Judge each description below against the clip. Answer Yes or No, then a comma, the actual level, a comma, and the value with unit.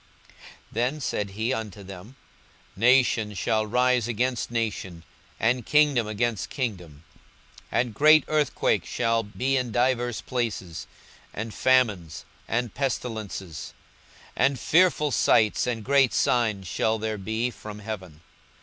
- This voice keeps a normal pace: No, slow, 125 wpm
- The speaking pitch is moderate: No, low, 115 Hz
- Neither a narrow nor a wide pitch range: Yes, average, 3.3 semitones